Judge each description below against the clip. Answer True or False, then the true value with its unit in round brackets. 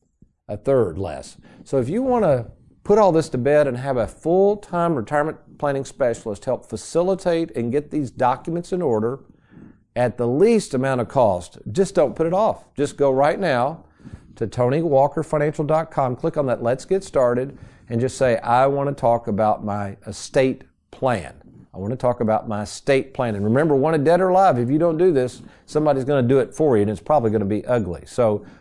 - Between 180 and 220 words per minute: True (205 wpm)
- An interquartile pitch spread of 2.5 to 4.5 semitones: False (5.2 semitones)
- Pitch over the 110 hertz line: True (135 Hz)